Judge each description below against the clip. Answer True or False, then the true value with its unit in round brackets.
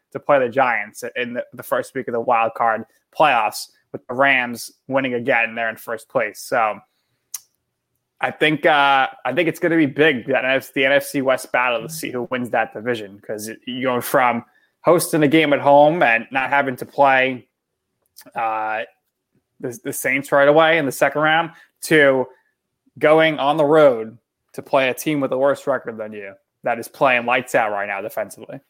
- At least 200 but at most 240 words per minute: False (190 wpm)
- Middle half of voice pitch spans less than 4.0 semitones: True (3.3 semitones)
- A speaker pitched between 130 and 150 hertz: True (135 Hz)